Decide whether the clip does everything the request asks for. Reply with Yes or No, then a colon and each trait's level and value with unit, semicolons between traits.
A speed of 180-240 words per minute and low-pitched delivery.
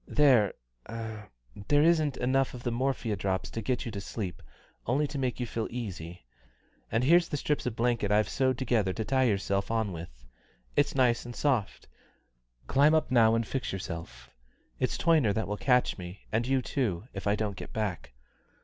Yes: average, 185 wpm; low, 115 Hz